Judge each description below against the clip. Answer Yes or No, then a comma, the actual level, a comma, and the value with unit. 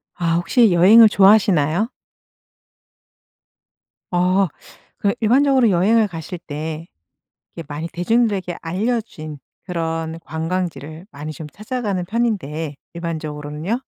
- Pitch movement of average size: Yes, average, 4.9 semitones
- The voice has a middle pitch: Yes, medium, 175 Hz